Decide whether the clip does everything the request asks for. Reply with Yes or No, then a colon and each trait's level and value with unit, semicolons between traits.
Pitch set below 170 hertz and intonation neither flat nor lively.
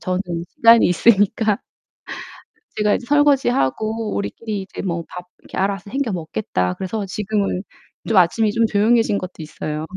No: high, 205 Hz; average, 3.6 semitones